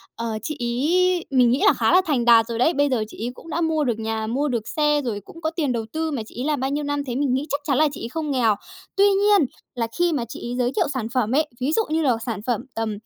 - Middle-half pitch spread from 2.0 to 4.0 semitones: No, average, 4.7 semitones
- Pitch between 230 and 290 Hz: Yes, very high, 270 Hz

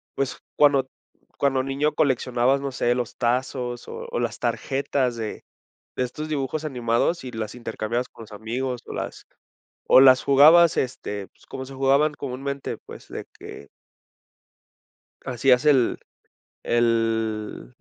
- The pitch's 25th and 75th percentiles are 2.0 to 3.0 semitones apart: Yes, average, 2.7 semitones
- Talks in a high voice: No, low, 130 Hz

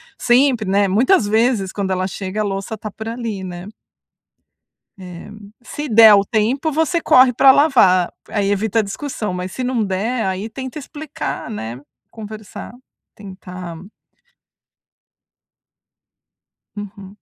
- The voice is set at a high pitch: Yes, high, 215 Hz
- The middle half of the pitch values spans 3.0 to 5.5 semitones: Yes, average, 4.6 semitones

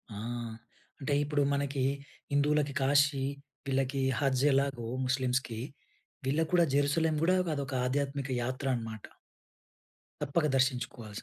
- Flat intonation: Yes, narrow, 1.9 semitones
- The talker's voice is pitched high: No, medium, 140 Hz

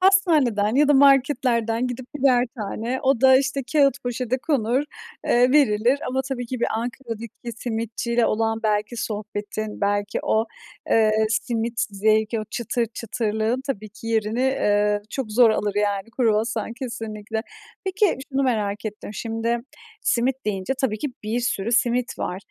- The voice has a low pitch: No, high, 230 Hz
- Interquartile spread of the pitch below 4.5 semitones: Yes, average, 3.1 semitones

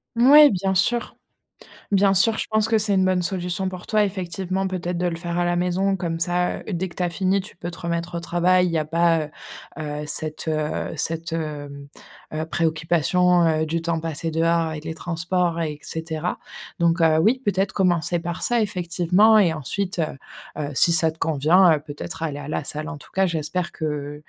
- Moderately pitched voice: Yes, medium, 170 Hz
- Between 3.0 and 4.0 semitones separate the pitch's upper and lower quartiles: No, narrow, 2.6 semitones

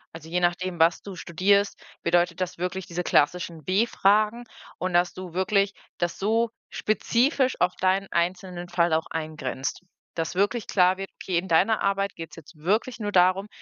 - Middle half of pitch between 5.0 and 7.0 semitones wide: No, narrow, 2.6 semitones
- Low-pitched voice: No, medium, 185 Hz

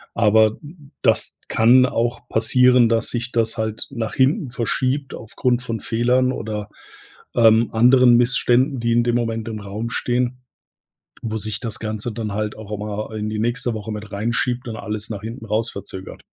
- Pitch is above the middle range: No, low, 115 Hz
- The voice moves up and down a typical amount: No, narrow, 2.3 semitones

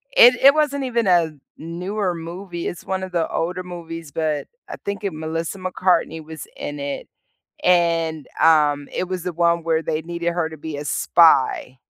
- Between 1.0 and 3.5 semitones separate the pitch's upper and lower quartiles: Yes, narrow, 2.4 semitones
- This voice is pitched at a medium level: Yes, medium, 170 Hz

